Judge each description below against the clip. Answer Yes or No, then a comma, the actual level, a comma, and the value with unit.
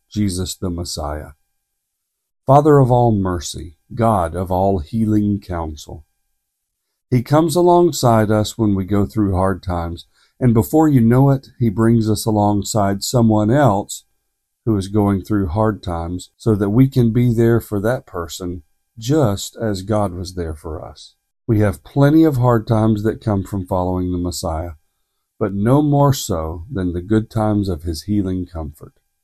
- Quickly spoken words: No, average, 160 wpm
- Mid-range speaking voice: No, low, 105 Hz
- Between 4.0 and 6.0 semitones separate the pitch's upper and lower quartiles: Yes, average, 4.3 semitones